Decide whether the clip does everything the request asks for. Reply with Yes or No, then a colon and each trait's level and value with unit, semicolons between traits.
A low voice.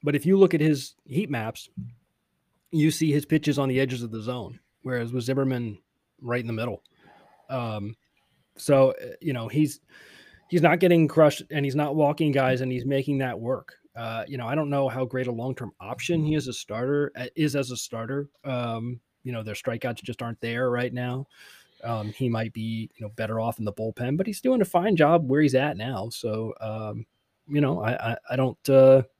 Yes: low, 130 Hz